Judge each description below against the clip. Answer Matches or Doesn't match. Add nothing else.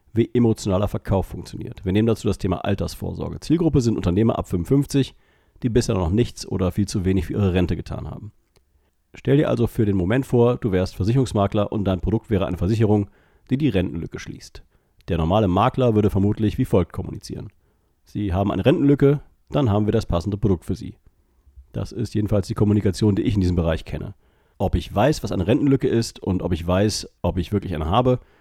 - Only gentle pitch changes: Doesn't match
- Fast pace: Matches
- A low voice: Matches